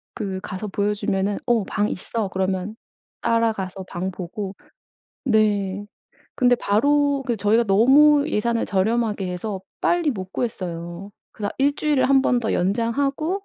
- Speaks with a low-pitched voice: No, high, 210 Hz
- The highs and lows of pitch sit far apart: No, average, 4.4 semitones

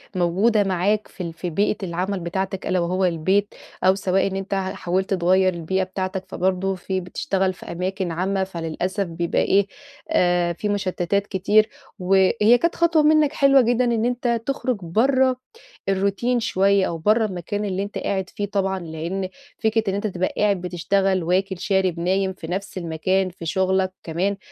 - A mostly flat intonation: Yes, narrow, 2.1 semitones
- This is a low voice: No, high, 190 Hz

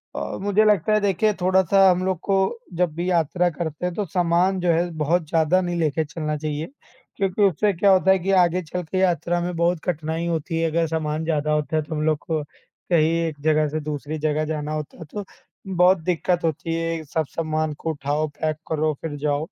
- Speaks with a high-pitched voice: No, medium, 165 Hz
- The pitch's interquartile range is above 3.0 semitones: No, average, 2.7 semitones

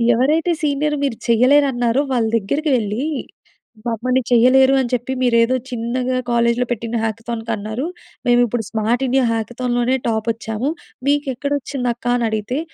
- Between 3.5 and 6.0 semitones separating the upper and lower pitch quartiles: No, narrow, 2.4 semitones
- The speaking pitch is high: Yes, high, 245 Hz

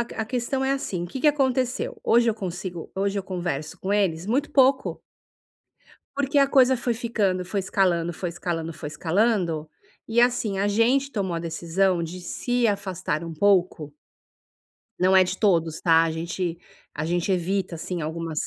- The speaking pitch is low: No, high, 190 Hz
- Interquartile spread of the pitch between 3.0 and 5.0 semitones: No, wide, 5.6 semitones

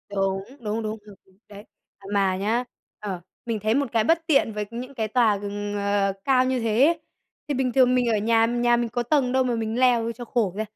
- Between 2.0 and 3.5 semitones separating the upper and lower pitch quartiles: Yes, average, 3.2 semitones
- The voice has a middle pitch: No, high, 230 Hz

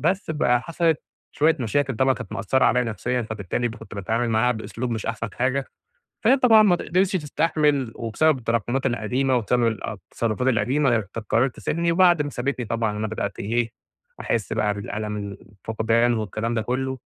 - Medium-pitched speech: No, low, 120 Hz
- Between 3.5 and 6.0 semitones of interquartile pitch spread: Yes, average, 4.0 semitones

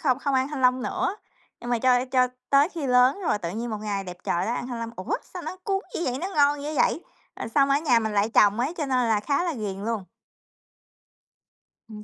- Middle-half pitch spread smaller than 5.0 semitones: Yes, average, 4.5 semitones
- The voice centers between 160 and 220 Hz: No, very high, 250 Hz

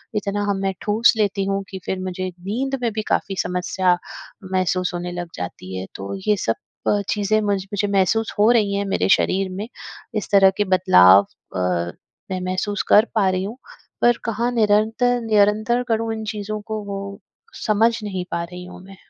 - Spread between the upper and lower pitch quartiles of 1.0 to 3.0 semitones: Yes, narrow, 2.6 semitones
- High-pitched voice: Yes, high, 200 Hz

